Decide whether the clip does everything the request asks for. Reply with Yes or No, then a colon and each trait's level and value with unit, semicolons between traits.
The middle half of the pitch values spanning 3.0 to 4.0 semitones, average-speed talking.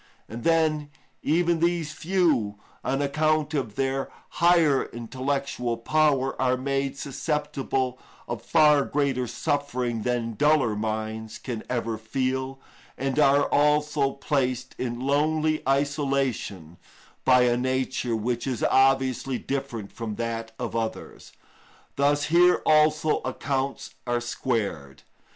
No: average, 3.6 semitones; slow, 115 wpm